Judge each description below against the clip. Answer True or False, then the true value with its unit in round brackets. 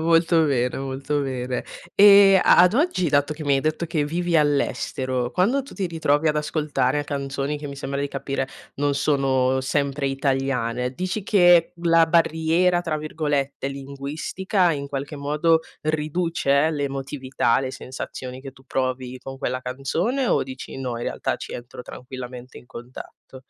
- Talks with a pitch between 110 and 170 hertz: True (140 Hz)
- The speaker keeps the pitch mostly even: False (3.5 semitones)